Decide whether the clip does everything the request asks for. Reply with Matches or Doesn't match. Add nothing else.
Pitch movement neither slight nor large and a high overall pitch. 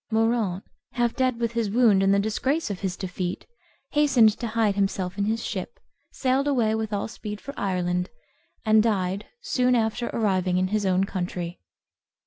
Matches